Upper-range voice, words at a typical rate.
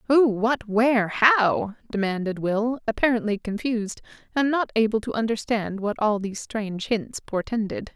No: high, 220 Hz; slow, 120 wpm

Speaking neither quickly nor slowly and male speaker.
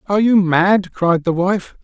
Yes: average, 195 wpm; male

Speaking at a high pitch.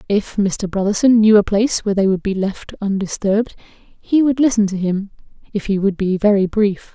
Yes: high, 205 Hz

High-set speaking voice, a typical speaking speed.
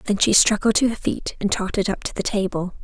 No: high, 200 Hz; fast, 255 wpm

